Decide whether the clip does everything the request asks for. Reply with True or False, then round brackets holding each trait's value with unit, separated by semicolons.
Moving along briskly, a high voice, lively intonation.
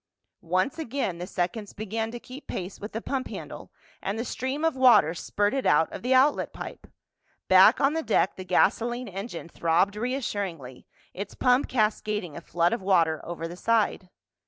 False (175 wpm; 210 Hz; 5.9 semitones)